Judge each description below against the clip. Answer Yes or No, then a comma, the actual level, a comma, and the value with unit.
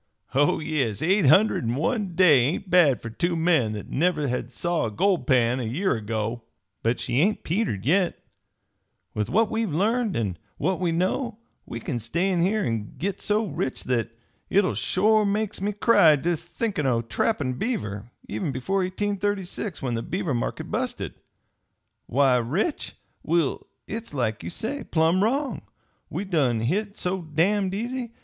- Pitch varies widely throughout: Yes, wide, 8.1 semitones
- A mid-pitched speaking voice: Yes, medium, 170 Hz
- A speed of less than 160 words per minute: No, average, 165 wpm